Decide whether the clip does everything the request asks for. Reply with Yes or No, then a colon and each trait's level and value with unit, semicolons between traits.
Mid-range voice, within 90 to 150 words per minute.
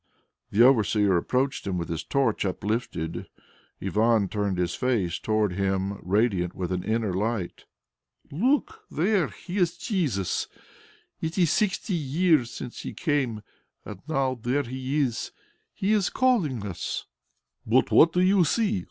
No: low, 120 Hz; average, 145 wpm